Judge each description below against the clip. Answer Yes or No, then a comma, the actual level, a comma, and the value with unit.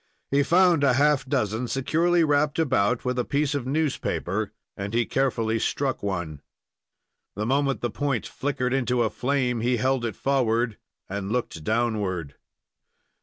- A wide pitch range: No, average, 4.3 semitones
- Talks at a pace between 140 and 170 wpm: Yes, average, 150 wpm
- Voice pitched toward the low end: Yes, low, 125 Hz